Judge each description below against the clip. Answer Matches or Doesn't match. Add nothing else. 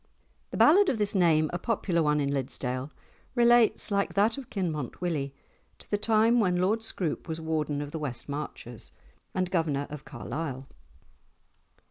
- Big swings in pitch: Matches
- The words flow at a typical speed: Matches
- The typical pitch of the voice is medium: Matches